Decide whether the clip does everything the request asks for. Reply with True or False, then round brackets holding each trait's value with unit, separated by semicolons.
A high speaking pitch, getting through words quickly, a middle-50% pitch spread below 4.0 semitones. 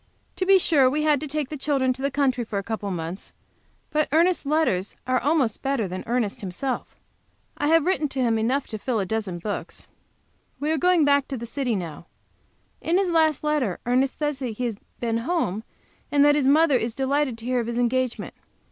False (265 Hz; 210 wpm; 4.8 semitones)